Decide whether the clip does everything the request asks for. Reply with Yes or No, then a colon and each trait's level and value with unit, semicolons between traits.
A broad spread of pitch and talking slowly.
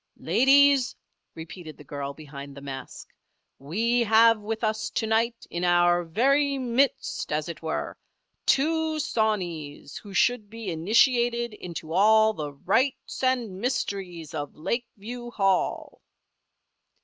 Yes: wide, 6.6 semitones; slow, 125 wpm